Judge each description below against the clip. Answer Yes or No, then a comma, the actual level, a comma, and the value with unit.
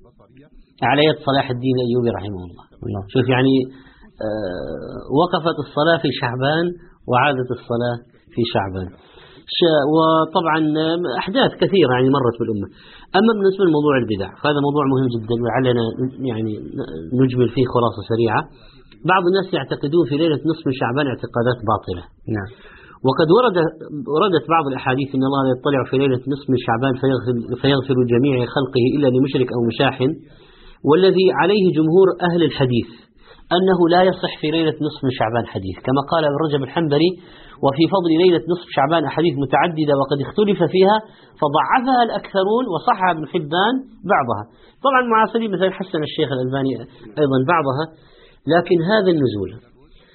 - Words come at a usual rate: Yes, average, 135 wpm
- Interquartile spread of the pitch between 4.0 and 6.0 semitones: Yes, average, 5.2 semitones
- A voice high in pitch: No, medium, 140 Hz